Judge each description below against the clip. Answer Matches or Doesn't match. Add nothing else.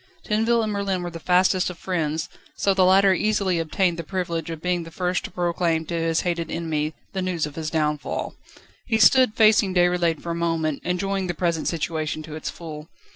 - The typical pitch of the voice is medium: Matches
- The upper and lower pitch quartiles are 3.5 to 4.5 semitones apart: Doesn't match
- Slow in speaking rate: Doesn't match